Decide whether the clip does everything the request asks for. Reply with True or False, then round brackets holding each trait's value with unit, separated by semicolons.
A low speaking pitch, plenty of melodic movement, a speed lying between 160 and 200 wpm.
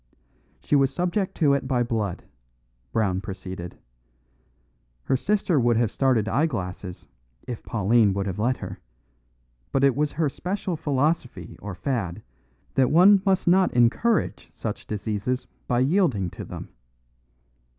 False (125 Hz; 7.0 semitones; 135 wpm)